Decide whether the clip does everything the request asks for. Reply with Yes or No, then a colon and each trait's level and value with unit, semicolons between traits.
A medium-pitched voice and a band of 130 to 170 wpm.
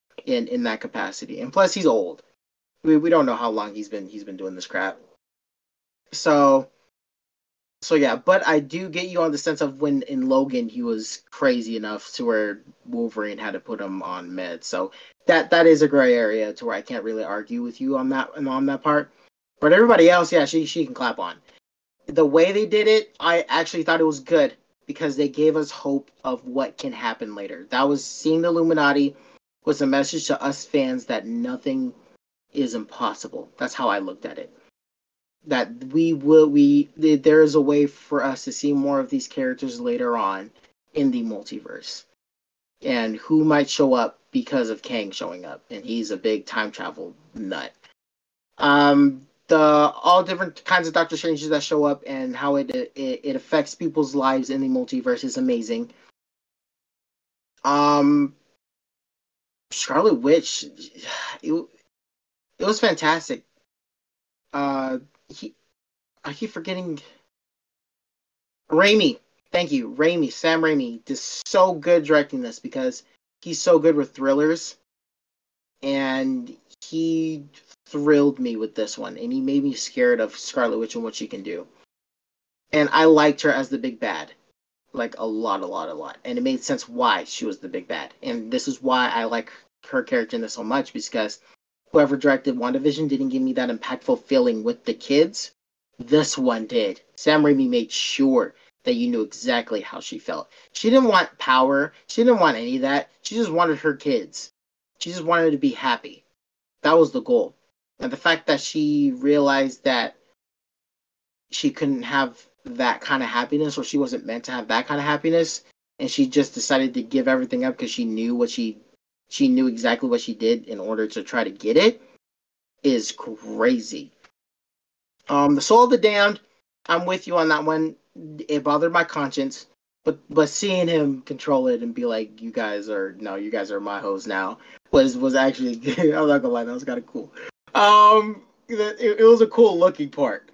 No: medium, 160 Hz; average, 185 wpm